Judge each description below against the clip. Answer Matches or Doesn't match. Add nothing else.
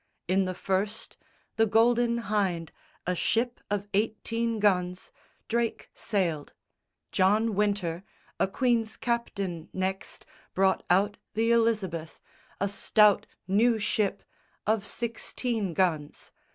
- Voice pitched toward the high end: Matches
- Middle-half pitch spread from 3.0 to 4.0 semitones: Matches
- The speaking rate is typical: Doesn't match